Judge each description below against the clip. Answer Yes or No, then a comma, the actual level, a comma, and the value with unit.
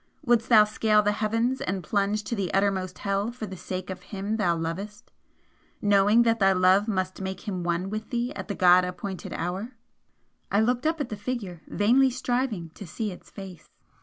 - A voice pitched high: Yes, high, 205 Hz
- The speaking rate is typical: Yes, average, 195 wpm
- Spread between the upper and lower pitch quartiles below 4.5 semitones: Yes, average, 3.3 semitones